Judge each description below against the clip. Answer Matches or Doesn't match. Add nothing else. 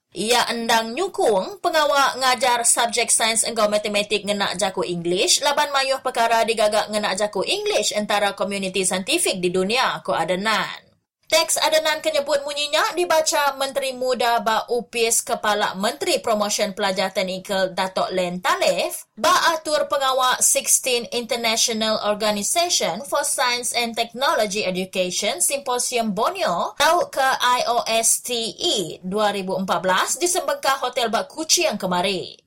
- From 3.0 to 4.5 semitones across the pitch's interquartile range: Doesn't match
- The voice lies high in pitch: Matches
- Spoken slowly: Matches